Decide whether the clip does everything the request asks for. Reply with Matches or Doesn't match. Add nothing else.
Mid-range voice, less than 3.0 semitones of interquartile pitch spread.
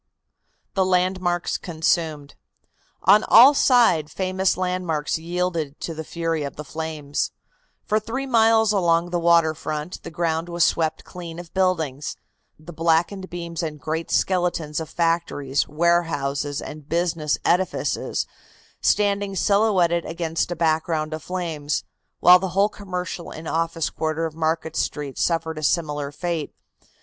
Matches